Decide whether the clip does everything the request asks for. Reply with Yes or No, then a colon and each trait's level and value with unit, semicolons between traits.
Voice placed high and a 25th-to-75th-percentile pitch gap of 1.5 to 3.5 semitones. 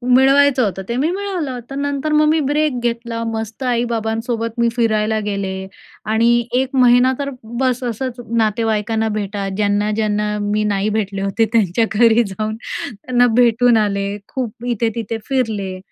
Yes: high, 230 Hz; average, 2.9 semitones